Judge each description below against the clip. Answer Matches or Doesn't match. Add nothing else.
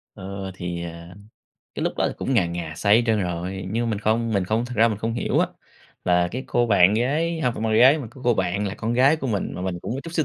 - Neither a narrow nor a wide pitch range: Matches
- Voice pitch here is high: Doesn't match